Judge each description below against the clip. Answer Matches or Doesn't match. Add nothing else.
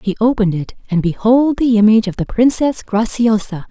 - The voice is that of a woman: Matches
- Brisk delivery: Doesn't match